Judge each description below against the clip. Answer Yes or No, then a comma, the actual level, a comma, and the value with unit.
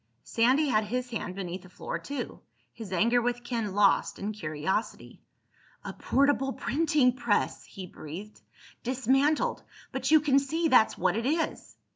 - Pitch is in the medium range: No, high, 240 Hz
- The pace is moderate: Yes, average, 145 wpm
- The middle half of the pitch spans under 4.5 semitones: No, average, 4.8 semitones